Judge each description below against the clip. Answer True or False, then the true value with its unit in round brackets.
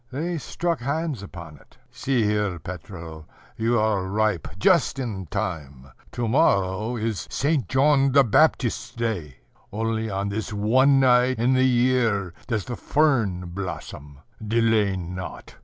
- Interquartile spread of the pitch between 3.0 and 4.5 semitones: False (5.4 semitones)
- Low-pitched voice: True (110 Hz)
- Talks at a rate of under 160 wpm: True (140 wpm)